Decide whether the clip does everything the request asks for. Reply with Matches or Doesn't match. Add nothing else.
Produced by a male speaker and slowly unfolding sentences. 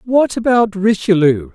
Matches